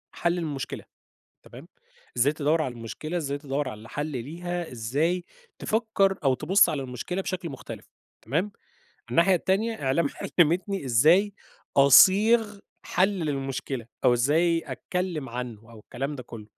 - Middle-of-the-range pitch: Yes, medium, 155 Hz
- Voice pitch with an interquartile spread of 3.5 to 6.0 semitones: Yes, wide, 5.5 semitones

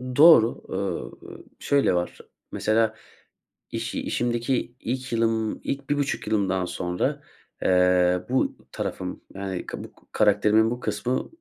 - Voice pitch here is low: Yes, low, 110 Hz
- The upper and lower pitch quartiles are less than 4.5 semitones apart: No, average, 4.8 semitones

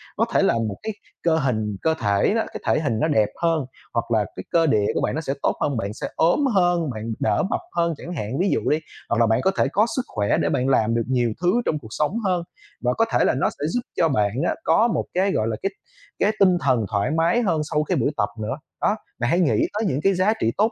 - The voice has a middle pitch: Yes, medium, 150 Hz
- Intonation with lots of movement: Yes, wide, 7.7 semitones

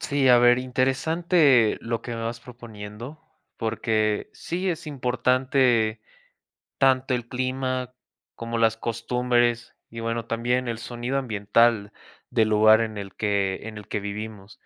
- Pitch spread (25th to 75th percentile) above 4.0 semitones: No, narrow, 2.6 semitones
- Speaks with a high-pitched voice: No, low, 120 Hz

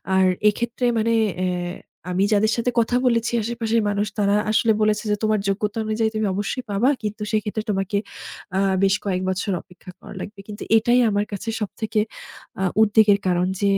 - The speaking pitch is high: Yes, high, 210 Hz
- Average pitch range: No, narrow, 2.0 semitones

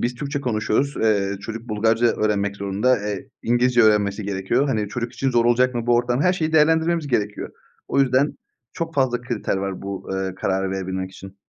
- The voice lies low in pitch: Yes, low, 115 Hz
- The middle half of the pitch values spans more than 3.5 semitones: Yes, average, 4.2 semitones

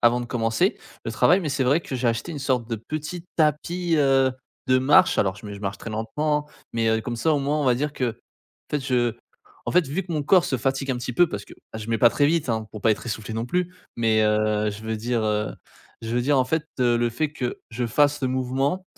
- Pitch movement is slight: No, average, 4.6 semitones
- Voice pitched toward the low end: Yes, low, 125 Hz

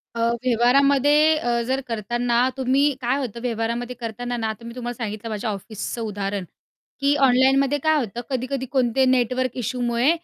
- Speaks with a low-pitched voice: No, high, 245 Hz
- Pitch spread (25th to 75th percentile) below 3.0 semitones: Yes, narrow, 2.4 semitones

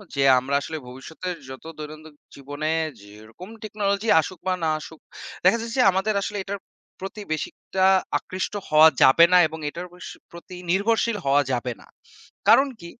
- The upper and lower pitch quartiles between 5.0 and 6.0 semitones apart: Yes, average, 5.3 semitones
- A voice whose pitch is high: No, medium, 170 Hz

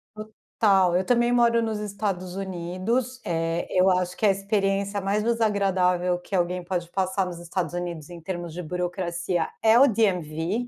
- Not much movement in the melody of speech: No, average, 3.1 semitones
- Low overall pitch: No, medium, 185 Hz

